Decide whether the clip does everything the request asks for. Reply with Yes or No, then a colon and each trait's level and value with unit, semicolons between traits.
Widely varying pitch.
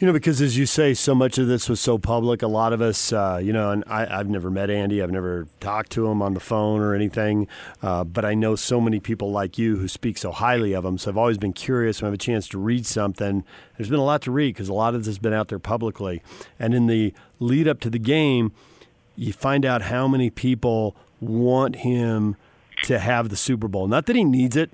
No: average, 3.3 semitones